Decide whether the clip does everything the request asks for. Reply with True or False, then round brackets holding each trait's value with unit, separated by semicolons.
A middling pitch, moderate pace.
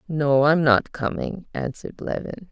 True (155 Hz; 145 wpm)